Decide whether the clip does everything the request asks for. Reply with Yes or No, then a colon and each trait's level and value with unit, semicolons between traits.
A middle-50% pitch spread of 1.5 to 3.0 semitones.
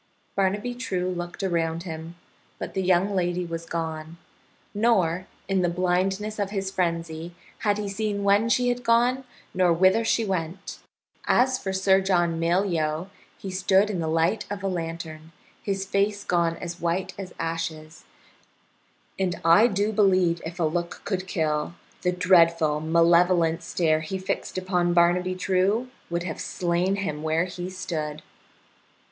Yes: average, 2.7 semitones